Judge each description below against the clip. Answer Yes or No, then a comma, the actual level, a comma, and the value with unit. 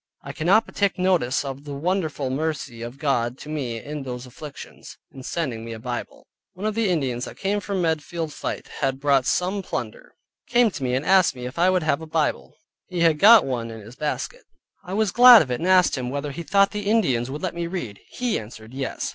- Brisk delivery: Yes, fast, 230 wpm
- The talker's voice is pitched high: No, medium, 150 Hz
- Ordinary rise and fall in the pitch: No, wide, 6.4 semitones